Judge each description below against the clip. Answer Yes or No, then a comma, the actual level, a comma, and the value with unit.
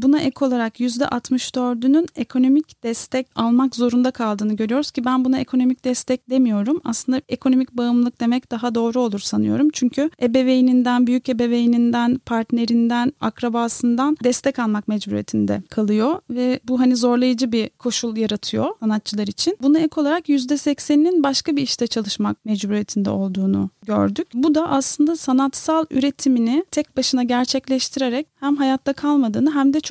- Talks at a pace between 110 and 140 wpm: Yes, average, 135 wpm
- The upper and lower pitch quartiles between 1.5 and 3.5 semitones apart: Yes, average, 2.7 semitones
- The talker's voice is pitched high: Yes, very high, 255 Hz